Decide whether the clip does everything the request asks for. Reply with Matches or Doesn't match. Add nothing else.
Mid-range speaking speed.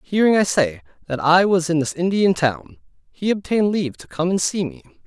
Doesn't match